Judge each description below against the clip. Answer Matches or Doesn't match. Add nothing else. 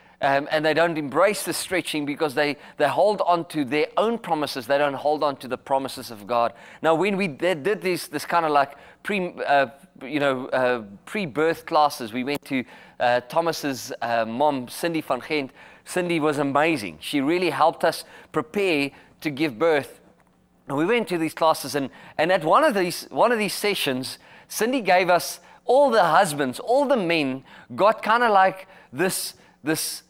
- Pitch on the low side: Doesn't match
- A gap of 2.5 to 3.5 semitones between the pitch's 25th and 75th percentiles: Doesn't match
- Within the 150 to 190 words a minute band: Matches